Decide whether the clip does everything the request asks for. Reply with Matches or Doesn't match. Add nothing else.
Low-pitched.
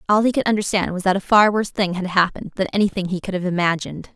Doesn't match